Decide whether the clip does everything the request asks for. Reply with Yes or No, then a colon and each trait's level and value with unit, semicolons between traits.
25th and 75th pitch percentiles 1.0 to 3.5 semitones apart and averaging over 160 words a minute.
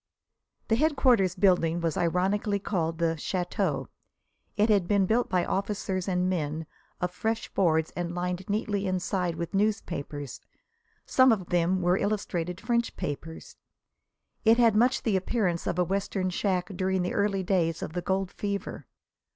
No: average, 2.8 semitones; average, 150 wpm